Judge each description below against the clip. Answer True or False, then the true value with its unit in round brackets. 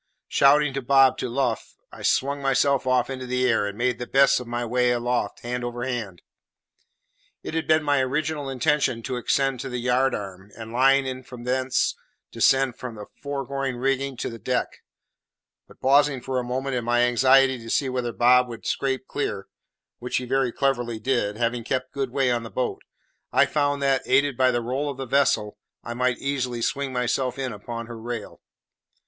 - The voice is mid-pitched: False (125 Hz)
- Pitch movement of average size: False (2.0 semitones)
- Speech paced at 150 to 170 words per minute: False (190 wpm)